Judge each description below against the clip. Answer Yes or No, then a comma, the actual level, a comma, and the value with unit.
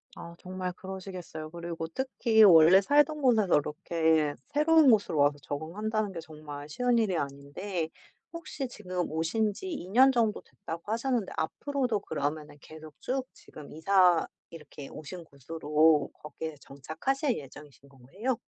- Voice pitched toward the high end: No, medium, 175 Hz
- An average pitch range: No, wide, 6.4 semitones